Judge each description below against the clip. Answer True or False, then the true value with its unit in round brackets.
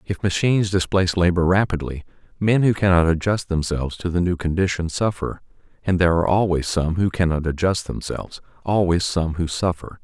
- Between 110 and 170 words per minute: True (165 wpm)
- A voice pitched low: True (90 Hz)